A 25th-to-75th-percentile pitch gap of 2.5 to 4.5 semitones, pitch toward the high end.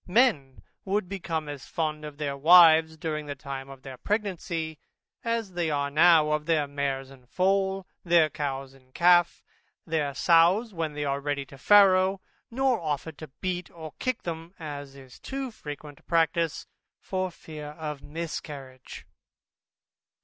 No: average, 3.9 semitones; medium, 160 Hz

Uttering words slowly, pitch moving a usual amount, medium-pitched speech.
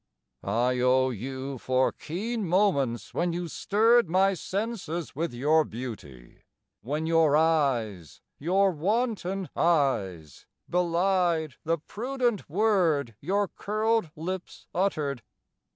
No: slow, 105 wpm; wide, 6.6 semitones; medium, 165 Hz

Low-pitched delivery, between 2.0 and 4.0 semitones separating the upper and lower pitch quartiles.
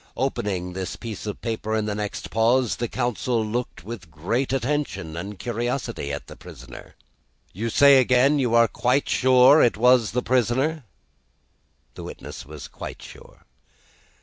Yes: low, 115 Hz; average, 3.7 semitones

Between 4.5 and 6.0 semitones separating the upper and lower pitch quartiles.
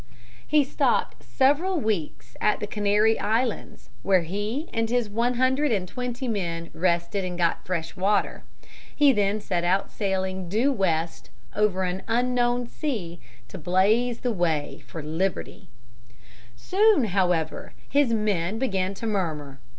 Yes: wide, 5.4 semitones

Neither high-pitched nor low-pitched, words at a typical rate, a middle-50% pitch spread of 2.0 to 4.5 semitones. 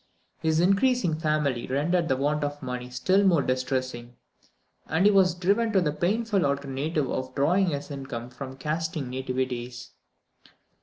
No: medium, 145 Hz; average, 145 wpm; average, 5.1 semitones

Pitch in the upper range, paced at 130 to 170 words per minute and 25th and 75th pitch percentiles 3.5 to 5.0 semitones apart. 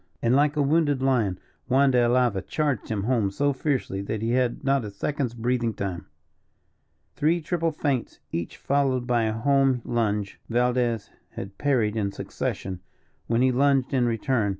No: low, 125 Hz; average, 165 wpm; average, 3.9 semitones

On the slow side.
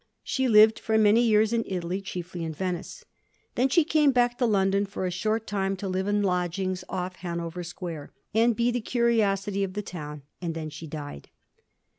No: average, 190 wpm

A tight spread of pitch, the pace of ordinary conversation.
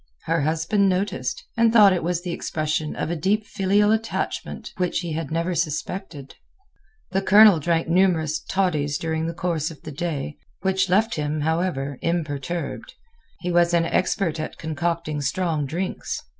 No: average, 3.3 semitones; average, 155 wpm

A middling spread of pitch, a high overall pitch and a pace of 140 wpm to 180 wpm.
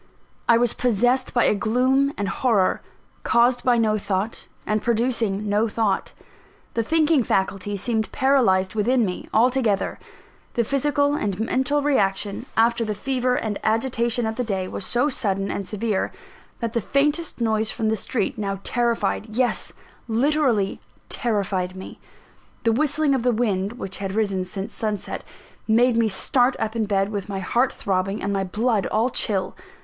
Yes: average, 3.7 semitones; high, 225 Hz; average, 160 wpm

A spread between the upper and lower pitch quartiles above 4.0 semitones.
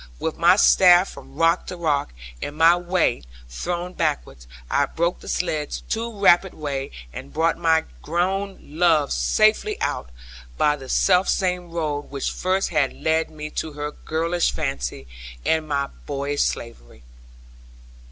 No: average, 3.5 semitones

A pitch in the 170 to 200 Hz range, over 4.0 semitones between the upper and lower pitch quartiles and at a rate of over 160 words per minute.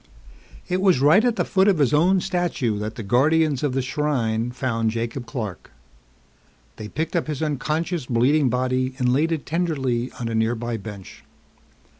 No: low, 135 Hz; average, 5.2 semitones; average, 170 wpm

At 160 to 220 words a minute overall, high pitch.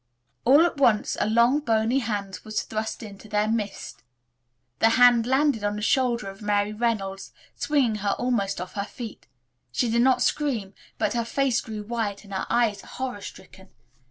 Yes: average, 175 wpm; high, 225 Hz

